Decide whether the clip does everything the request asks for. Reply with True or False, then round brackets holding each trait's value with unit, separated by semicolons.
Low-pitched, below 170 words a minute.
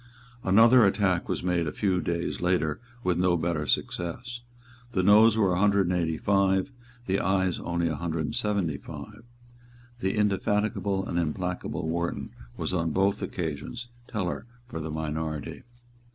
True (90 Hz; 150 wpm)